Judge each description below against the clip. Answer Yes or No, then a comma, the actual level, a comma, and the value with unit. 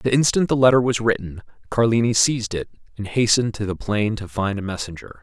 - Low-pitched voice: Yes, low, 110 Hz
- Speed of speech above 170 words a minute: Yes, fast, 205 wpm